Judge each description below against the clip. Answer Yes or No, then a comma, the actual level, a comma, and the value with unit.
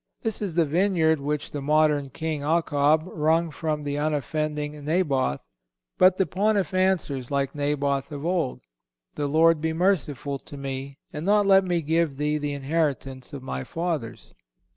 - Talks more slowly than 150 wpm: No, average, 160 wpm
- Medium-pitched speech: Yes, medium, 150 Hz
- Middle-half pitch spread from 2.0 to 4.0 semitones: Yes, average, 2.9 semitones